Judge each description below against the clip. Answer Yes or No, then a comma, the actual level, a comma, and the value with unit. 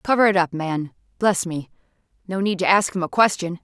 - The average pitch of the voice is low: No, medium, 185 Hz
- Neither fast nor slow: Yes, average, 180 wpm